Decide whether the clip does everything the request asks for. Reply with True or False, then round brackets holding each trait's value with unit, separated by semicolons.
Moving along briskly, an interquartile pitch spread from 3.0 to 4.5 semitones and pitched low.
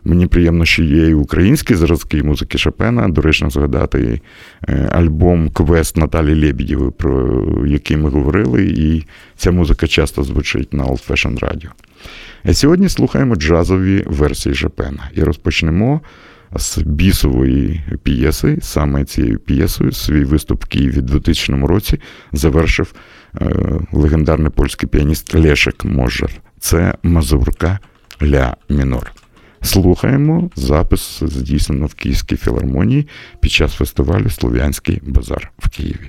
False (120 wpm; 3.4 semitones; 80 Hz)